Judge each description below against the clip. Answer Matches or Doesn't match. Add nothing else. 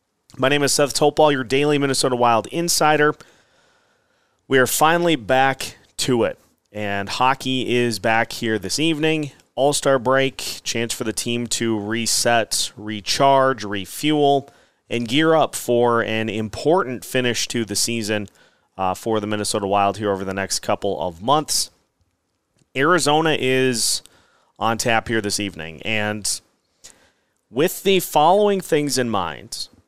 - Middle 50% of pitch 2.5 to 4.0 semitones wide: Doesn't match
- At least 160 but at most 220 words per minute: Doesn't match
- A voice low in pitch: Matches